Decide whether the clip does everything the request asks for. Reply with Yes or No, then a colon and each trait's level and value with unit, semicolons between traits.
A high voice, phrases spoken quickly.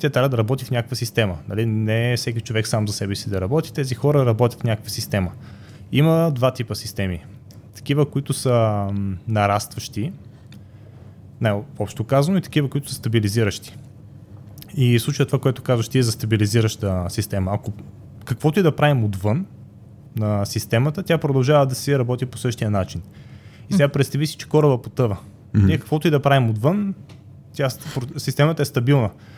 No: low, 120 Hz; fast, 170 wpm